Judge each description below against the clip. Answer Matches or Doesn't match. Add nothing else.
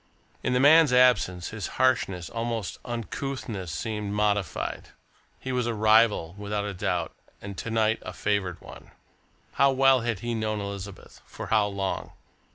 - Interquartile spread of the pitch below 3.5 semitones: Matches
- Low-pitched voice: Matches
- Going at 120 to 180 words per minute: Matches